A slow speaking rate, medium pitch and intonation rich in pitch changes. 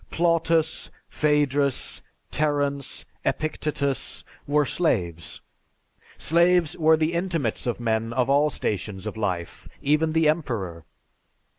Yes: slow, 105 wpm; medium, 145 Hz; wide, 5.9 semitones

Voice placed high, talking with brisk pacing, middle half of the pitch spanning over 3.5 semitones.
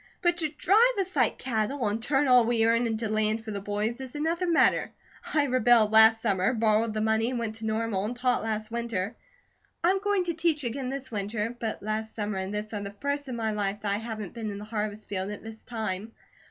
No: high, 225 Hz; fast, 230 wpm; average, 3.2 semitones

